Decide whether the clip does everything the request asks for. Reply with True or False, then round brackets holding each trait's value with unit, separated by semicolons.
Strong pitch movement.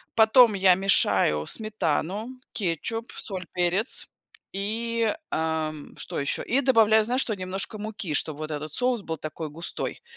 True (5.7 semitones)